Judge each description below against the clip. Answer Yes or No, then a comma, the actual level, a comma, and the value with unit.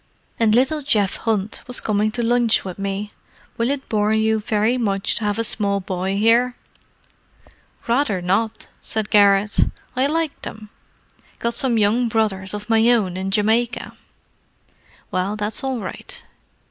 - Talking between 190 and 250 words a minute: No, average, 145 wpm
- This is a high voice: Yes, high, 215 Hz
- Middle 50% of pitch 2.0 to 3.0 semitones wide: Yes, average, 2.7 semitones